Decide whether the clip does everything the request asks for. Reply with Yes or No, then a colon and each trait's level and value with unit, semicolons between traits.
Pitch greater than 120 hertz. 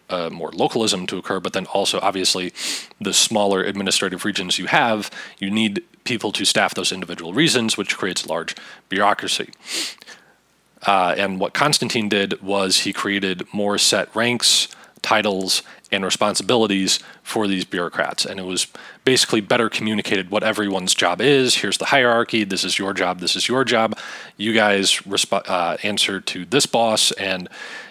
No: low, 100 Hz